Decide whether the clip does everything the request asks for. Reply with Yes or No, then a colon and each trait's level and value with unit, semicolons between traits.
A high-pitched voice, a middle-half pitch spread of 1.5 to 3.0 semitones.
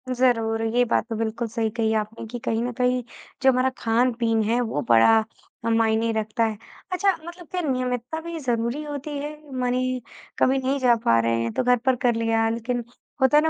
Yes: high, 240 Hz; narrow, 2.4 semitones